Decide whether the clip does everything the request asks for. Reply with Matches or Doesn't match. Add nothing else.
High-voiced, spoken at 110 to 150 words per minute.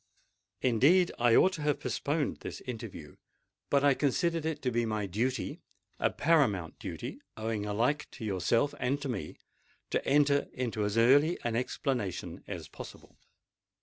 Doesn't match